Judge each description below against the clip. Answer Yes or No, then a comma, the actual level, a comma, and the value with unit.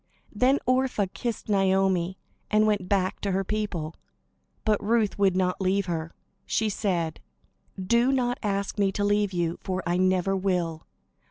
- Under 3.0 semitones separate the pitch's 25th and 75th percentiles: Yes, narrow, 2.5 semitones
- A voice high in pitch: Yes, high, 195 Hz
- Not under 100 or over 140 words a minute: No, average, 155 wpm